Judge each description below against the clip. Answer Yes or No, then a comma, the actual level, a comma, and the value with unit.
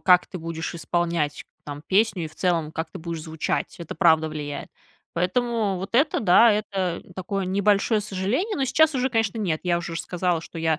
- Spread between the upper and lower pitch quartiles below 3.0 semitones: No, average, 4.3 semitones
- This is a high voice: No, medium, 180 Hz